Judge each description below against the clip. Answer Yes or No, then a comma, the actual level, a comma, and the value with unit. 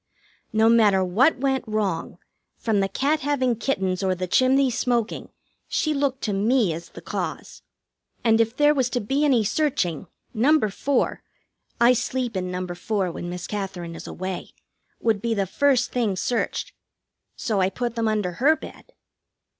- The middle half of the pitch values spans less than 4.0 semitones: No, average, 5.2 semitones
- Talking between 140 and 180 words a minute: Yes, average, 165 wpm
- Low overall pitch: No, high, 225 Hz